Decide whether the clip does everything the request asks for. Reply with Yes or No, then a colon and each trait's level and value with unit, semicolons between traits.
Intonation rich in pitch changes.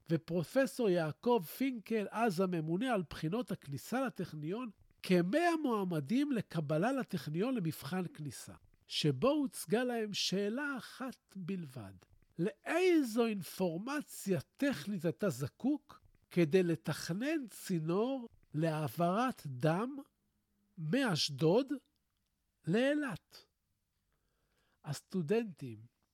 Yes: wide, 7.4 semitones